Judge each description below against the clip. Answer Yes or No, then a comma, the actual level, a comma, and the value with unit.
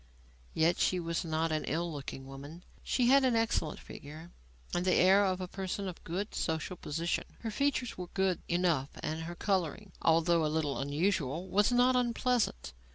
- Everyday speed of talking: Yes, average, 175 wpm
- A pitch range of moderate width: Yes, average, 4.0 semitones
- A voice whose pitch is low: No, medium, 175 Hz